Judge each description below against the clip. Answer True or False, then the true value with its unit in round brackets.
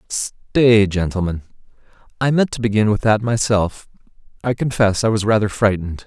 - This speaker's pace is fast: False (150 wpm)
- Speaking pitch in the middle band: False (110 Hz)